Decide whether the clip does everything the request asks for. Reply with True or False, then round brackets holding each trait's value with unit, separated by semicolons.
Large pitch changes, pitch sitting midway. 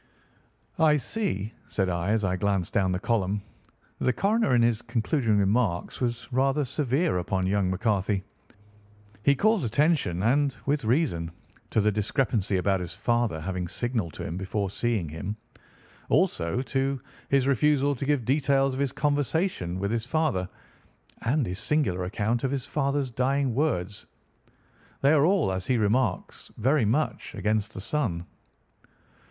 False (6.2 semitones; 115 Hz)